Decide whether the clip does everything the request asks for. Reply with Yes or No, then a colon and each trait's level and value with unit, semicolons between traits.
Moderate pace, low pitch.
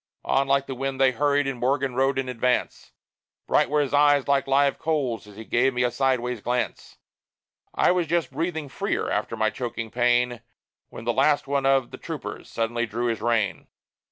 Yes: average, 190 wpm; low, 130 Hz